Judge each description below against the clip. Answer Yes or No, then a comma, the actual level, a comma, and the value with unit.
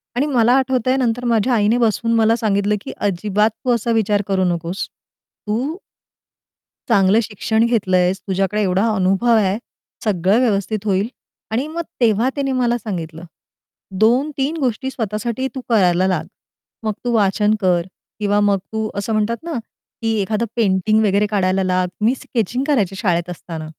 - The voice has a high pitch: Yes, high, 215 Hz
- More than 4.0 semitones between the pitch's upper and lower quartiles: No, average, 3.5 semitones